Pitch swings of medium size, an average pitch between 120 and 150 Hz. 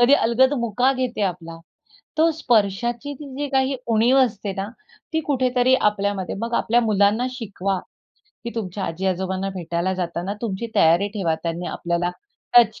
No: average, 4.9 semitones; high, 210 Hz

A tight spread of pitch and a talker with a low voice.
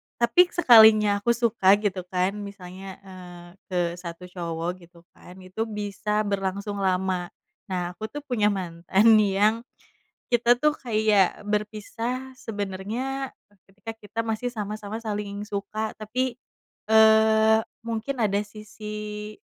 No: narrow, 2.3 semitones; high, 210 Hz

